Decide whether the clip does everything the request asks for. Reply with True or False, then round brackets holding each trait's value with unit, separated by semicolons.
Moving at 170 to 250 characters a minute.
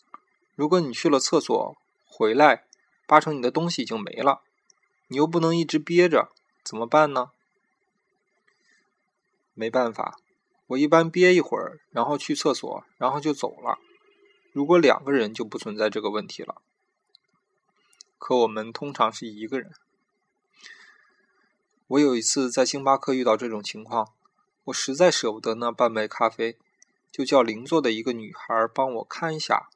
True (230 characters per minute)